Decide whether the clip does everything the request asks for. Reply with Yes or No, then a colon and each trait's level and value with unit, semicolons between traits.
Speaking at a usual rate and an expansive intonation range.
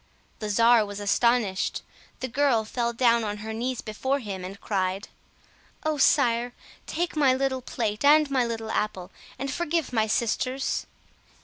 No: average, 150 wpm; average, 3.8 semitones